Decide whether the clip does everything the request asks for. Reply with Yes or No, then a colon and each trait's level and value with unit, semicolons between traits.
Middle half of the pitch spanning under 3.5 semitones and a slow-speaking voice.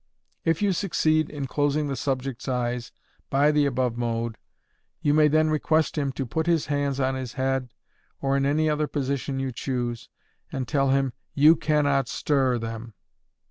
No: average, 2.8 semitones; average, 175 wpm